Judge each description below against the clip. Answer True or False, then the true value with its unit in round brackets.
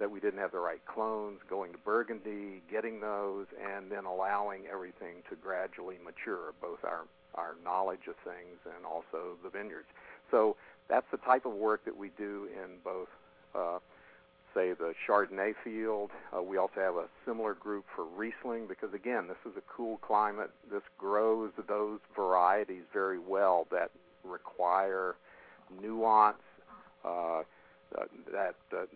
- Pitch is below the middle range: True (105 Hz)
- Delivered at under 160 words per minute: True (150 wpm)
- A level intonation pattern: True (2.1 semitones)